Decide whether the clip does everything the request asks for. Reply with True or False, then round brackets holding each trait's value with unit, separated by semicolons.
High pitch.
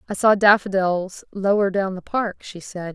True (195 Hz)